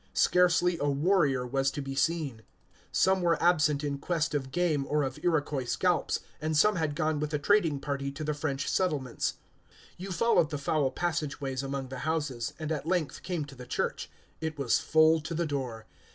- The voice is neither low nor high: Yes, medium, 150 Hz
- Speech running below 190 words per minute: No, average, 195 wpm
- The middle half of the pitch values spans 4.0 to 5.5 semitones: No, average, 3.3 semitones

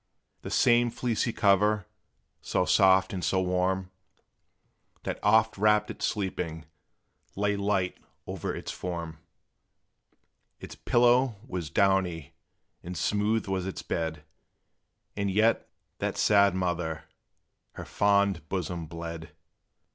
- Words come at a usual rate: No, slow, 110 wpm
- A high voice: No, very low, 95 Hz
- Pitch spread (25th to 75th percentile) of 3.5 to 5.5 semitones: No, average, 3.1 semitones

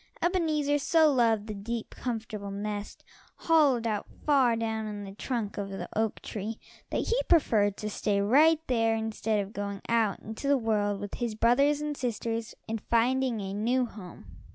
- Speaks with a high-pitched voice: Yes, high, 225 Hz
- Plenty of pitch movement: No, average, 3.9 semitones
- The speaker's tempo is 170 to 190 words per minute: Yes, average, 175 wpm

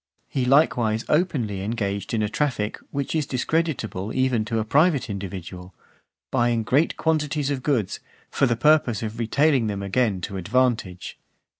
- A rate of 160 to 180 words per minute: No, average, 150 wpm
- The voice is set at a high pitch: No, low, 120 Hz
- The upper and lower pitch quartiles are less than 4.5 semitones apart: No, average, 5.3 semitones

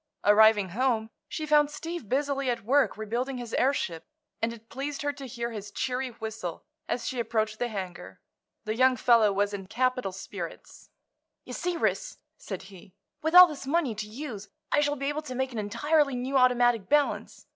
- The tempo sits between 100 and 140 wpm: No, average, 185 wpm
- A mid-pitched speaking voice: No, high, 245 Hz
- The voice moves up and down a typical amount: Yes, average, 4.4 semitones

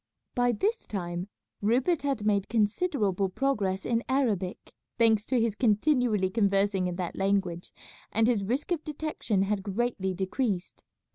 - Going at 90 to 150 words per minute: Yes, average, 140 wpm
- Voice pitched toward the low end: No, high, 210 Hz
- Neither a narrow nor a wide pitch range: Yes, average, 4.3 semitones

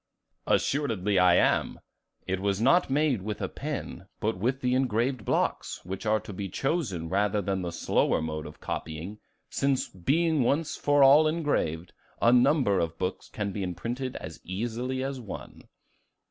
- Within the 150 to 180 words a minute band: Yes, average, 160 wpm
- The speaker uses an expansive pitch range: Yes, wide, 6.2 semitones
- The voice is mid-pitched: No, low, 110 Hz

